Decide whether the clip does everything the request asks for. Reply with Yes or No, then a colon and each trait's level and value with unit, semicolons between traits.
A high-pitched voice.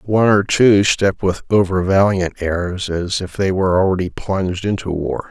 No: very low, 95 Hz